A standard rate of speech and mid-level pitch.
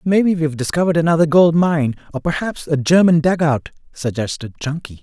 Yes: average, 155 wpm; medium, 155 Hz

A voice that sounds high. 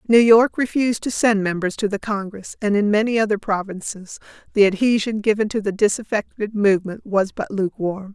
Yes: high, 205 Hz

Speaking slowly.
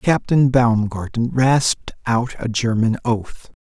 Yes: slow, 115 wpm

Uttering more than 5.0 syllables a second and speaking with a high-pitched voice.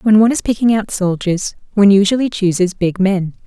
Yes: 5.8 syllables/s; high, 200 Hz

